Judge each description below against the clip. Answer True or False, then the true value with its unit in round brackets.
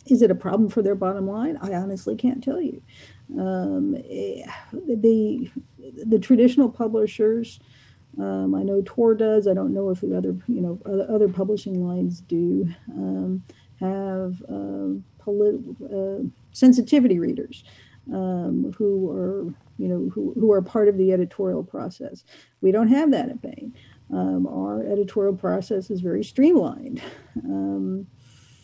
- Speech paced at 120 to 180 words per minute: True (145 wpm)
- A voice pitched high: True (195 Hz)